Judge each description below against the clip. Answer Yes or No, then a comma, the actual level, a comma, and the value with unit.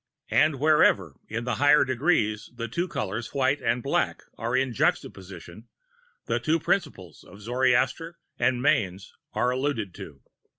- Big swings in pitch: No, average, 5.0 semitones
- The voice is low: Yes, low, 125 Hz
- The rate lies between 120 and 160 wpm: Yes, average, 140 wpm